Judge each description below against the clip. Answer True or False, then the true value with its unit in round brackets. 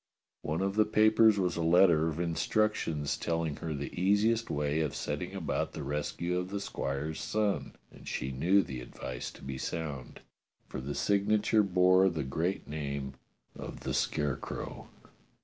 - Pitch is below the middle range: True (85 Hz)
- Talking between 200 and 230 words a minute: False (160 wpm)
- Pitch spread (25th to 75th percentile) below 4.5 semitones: False (5.3 semitones)